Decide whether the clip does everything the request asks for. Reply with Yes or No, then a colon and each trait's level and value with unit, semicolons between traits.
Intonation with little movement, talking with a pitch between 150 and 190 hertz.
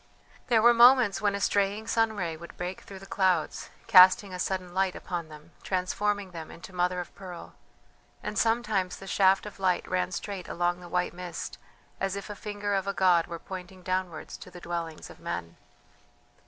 Yes: narrow, 2.3 semitones; medium, 185 Hz